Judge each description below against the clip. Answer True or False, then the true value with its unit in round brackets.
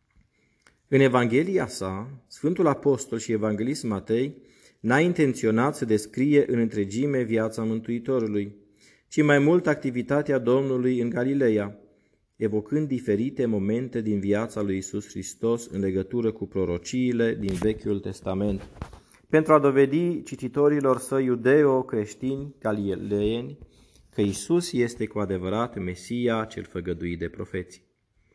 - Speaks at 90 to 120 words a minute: True (115 wpm)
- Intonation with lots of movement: False (4.3 semitones)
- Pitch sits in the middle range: False (115 Hz)